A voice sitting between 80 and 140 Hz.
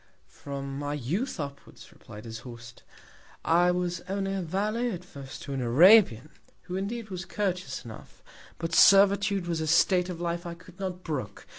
No: medium, 175 Hz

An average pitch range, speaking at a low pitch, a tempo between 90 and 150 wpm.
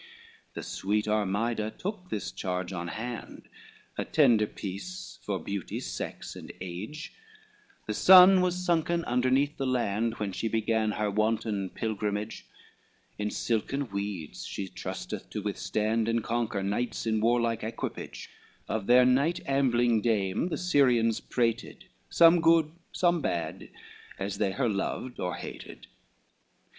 Yes: average, 4.5 semitones; low, 115 Hz; slow, 135 wpm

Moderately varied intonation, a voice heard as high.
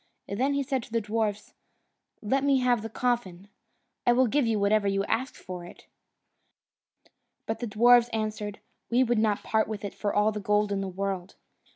Yes: average, 3.1 semitones; high, 215 Hz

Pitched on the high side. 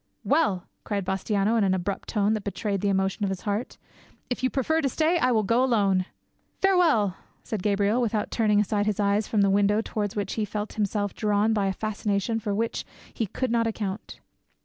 Yes: high, 210 Hz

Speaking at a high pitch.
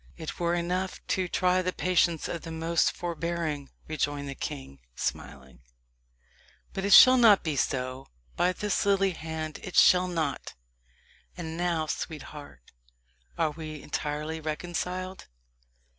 No: medium, 165 Hz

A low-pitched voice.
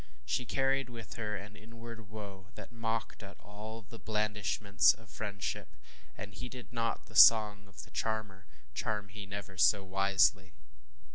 Yes: low, 105 Hz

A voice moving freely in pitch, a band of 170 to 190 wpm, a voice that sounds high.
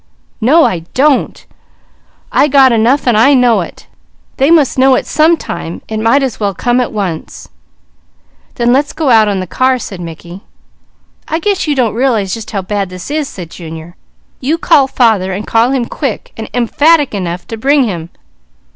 Yes: wide, 5.7 semitones; average, 180 wpm; high, 235 Hz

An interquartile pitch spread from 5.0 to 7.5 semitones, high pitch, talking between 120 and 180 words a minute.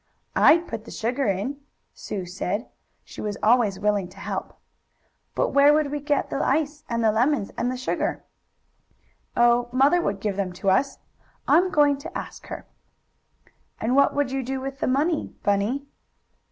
Yes: average, 5.3 semitones; very high, 255 Hz; average, 170 wpm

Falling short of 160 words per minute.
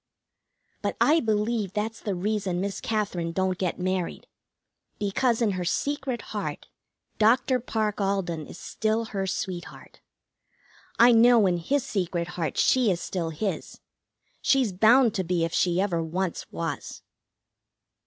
Yes: average, 140 wpm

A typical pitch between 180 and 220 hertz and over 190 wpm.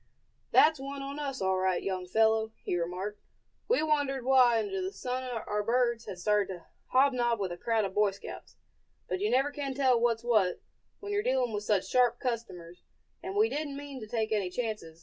No: high, 230 Hz; average, 200 wpm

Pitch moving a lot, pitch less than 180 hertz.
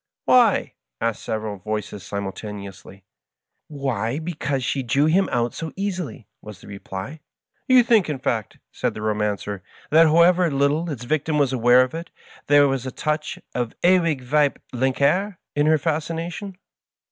Yes: wide, 6.5 semitones; medium, 140 Hz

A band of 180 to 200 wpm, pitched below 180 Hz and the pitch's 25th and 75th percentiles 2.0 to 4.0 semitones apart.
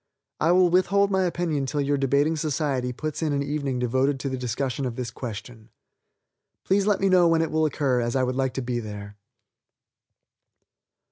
No: average, 190 wpm; medium, 140 Hz; average, 4.4 semitones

